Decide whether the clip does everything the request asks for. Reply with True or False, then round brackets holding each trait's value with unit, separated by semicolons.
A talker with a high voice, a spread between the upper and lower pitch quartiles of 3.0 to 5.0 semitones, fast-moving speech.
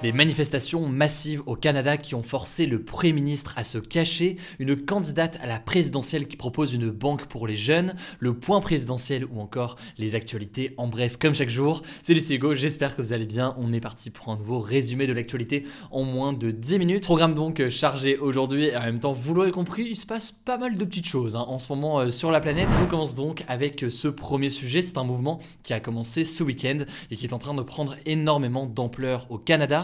False (140 Hz; 4.2 semitones; 225 wpm)